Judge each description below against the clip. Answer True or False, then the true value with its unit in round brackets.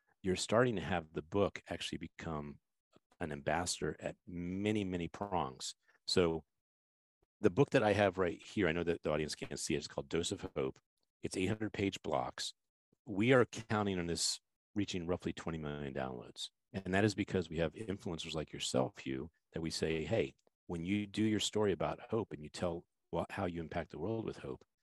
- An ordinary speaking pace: True (195 wpm)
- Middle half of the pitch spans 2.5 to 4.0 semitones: False (4.7 semitones)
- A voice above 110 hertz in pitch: False (85 Hz)